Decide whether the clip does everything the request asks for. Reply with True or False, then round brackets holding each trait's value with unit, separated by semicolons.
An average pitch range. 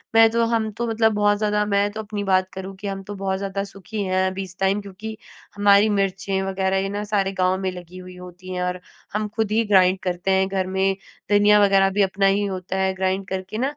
False (1.6 semitones)